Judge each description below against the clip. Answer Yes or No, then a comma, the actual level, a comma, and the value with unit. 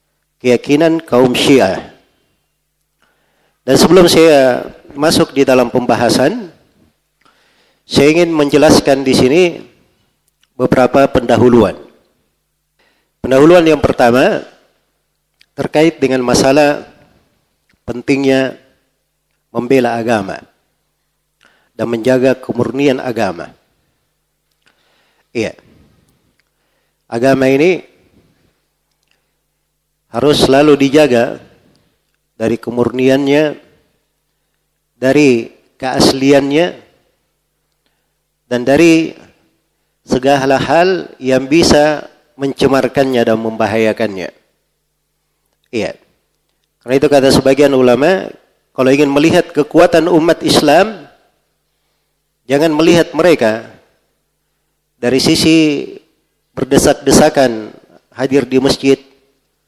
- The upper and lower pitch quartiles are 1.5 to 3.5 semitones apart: Yes, average, 3.1 semitones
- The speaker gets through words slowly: Yes, slow, 70 wpm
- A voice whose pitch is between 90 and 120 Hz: No, low, 135 Hz